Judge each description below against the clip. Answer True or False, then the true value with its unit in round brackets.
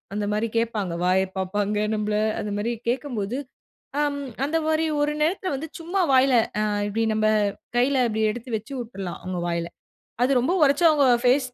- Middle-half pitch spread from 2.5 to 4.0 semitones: False (5.4 semitones)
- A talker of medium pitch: False (240 Hz)